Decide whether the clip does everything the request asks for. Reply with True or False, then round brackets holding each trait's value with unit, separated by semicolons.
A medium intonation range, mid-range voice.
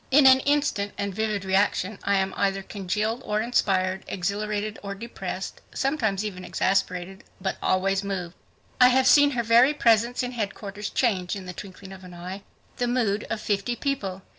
False (3.6 semitones; 205 Hz)